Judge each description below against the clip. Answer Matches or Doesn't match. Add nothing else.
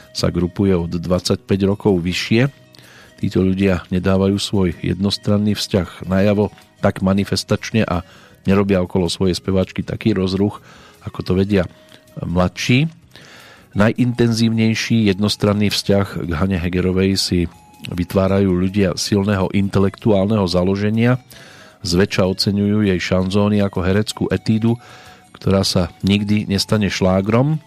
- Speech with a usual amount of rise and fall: Doesn't match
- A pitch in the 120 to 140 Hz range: Doesn't match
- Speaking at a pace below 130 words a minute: Matches